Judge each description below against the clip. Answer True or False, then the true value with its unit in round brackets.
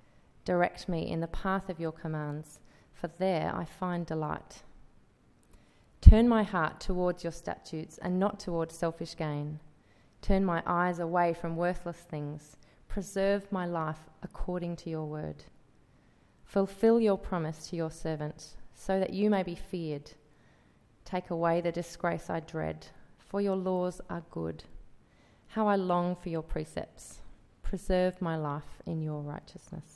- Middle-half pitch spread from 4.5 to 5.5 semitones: False (2.9 semitones)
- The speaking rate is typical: True (145 wpm)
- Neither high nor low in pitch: True (170 Hz)